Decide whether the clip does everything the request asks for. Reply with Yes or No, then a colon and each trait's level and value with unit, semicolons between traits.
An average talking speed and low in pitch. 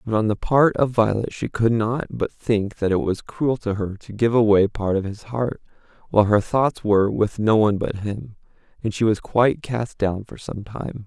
No: fast, 230 wpm; low, 110 Hz